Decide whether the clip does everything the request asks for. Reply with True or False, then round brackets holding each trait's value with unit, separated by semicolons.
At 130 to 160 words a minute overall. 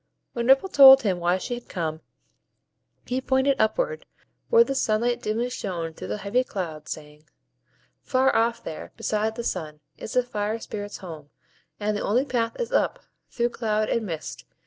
False (170 wpm)